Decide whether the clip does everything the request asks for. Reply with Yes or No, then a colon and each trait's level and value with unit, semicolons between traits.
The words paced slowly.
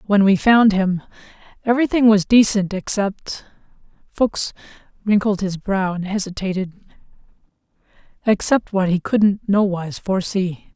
Yes: slow, 105 wpm